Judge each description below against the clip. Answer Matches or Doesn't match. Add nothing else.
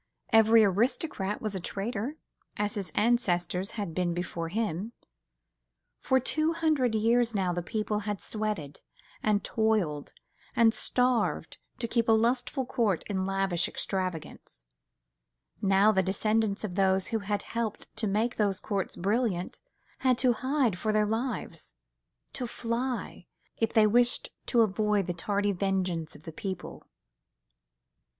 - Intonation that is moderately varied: Matches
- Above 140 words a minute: Doesn't match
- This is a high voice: Matches